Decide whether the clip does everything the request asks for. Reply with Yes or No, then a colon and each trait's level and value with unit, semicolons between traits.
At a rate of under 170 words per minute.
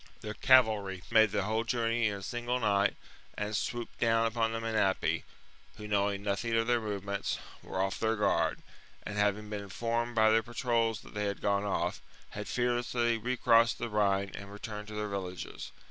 No: average, 190 wpm